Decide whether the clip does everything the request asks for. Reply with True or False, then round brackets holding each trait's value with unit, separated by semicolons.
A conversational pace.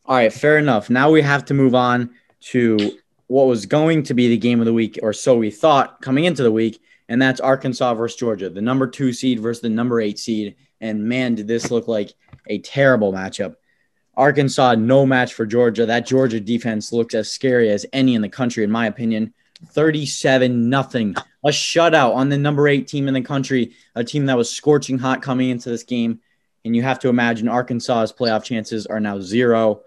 False (210 wpm)